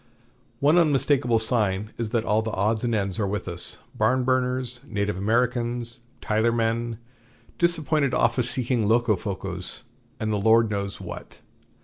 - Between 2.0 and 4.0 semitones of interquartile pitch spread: Yes, average, 2.9 semitones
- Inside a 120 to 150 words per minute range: Yes, slow, 135 wpm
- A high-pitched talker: No, low, 115 Hz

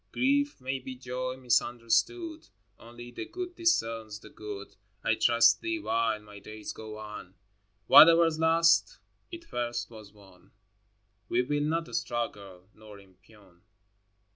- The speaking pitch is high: No, low, 120 Hz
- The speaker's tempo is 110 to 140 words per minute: Yes, slow, 135 wpm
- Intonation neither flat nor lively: No, wide, 7.4 semitones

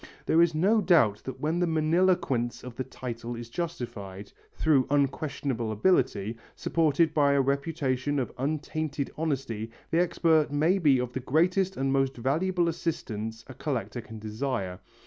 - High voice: No, medium, 140 Hz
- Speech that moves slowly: No, average, 150 wpm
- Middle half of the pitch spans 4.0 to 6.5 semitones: Yes, average, 5.1 semitones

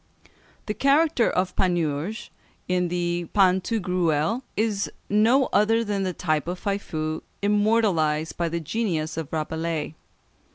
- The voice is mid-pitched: Yes, medium, 180 Hz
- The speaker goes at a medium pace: No, slow, 120 wpm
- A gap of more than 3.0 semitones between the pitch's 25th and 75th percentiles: Yes, average, 4.6 semitones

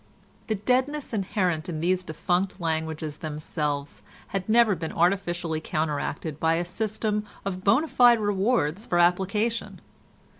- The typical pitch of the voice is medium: Yes, medium, 180 Hz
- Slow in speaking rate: Yes, slow, 125 wpm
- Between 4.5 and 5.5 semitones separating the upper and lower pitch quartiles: Yes, average, 4.8 semitones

